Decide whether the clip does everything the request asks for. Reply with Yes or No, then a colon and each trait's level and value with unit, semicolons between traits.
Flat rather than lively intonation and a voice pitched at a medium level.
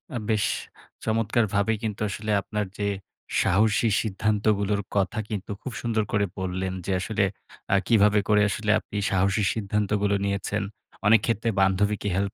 No: narrow, 1.6 semitones; low, 105 Hz